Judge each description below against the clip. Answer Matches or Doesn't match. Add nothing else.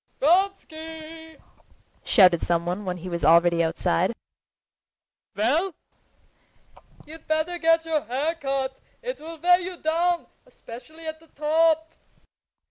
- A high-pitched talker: Matches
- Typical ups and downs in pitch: Doesn't match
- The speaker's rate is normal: Doesn't match